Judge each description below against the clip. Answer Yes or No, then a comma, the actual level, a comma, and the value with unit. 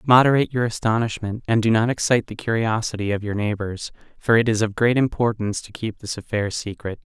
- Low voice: Yes, low, 110 Hz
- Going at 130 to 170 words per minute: No, average, 195 wpm